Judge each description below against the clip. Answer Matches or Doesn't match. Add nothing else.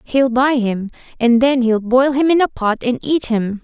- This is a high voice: Matches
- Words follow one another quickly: Matches